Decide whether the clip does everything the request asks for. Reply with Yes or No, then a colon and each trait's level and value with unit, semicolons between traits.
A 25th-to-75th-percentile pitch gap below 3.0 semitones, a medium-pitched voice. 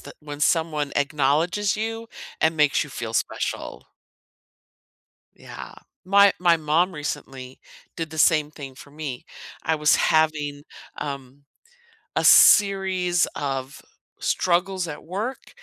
No: average, 3.9 semitones; medium, 155 Hz